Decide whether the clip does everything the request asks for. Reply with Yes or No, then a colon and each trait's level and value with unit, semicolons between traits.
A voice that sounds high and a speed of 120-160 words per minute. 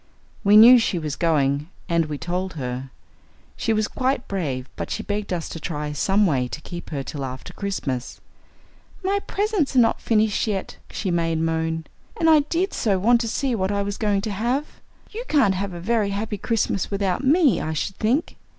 No: high, 200 Hz; average, 195 wpm